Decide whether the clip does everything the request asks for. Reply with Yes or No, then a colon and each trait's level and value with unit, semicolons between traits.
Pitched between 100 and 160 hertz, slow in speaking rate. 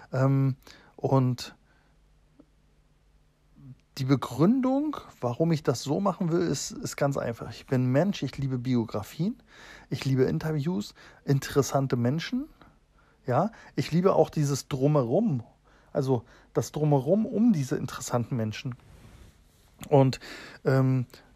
Yes: medium, 140 Hz; slow, 110 wpm